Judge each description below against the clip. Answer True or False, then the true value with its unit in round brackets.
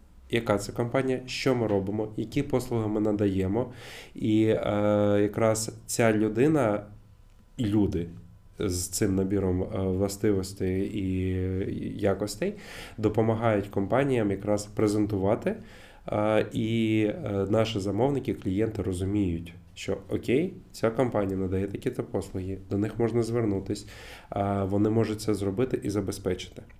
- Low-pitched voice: True (105 Hz)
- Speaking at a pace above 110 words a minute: False (105 wpm)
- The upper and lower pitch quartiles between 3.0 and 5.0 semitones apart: False (2.4 semitones)